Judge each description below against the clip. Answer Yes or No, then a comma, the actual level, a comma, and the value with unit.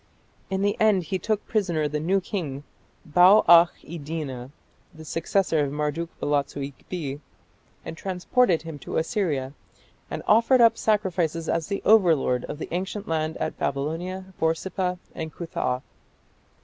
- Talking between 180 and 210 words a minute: No, average, 140 wpm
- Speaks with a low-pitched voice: No, medium, 165 Hz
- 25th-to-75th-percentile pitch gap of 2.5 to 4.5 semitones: Yes, average, 4.1 semitones